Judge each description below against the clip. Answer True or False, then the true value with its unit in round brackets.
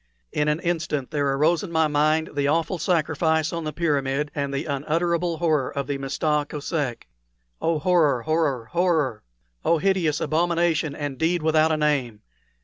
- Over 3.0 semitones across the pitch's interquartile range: False (2.7 semitones)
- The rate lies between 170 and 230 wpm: False (160 wpm)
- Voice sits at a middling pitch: True (155 Hz)